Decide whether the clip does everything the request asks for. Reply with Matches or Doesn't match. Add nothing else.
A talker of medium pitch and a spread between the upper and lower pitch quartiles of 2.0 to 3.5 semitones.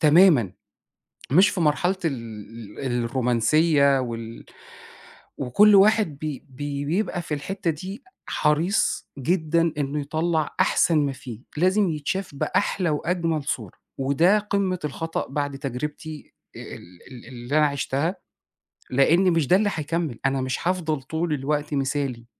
Doesn't match